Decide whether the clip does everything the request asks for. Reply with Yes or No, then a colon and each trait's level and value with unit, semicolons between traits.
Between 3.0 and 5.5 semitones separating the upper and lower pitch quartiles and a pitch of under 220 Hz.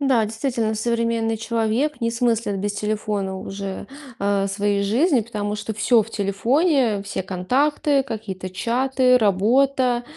No: average, 3.6 semitones; high, 225 Hz